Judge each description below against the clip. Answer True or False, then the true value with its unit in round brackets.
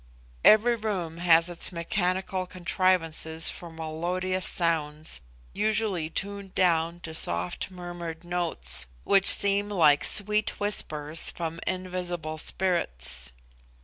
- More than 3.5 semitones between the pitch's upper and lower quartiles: False (2.7 semitones)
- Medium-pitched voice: True (175 Hz)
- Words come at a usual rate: False (105 wpm)